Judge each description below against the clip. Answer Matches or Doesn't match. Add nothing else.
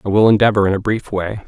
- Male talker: Matches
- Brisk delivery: Matches